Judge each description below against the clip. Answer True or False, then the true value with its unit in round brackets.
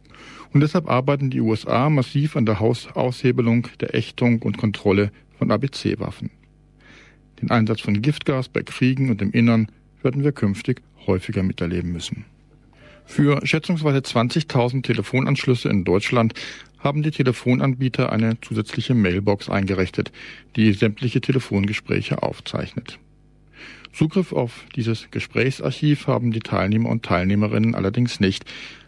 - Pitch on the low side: True (120 Hz)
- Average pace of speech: False (120 wpm)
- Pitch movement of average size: True (3.9 semitones)